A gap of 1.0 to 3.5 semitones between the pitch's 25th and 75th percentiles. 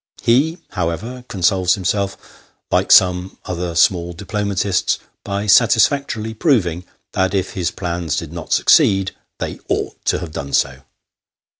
Yes: average, 3.2 semitones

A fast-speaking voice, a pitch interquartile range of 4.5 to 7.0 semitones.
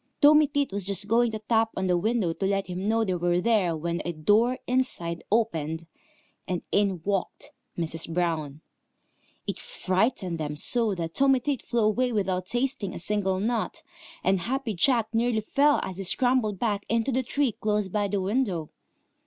No: average, 180 wpm; average, 4.9 semitones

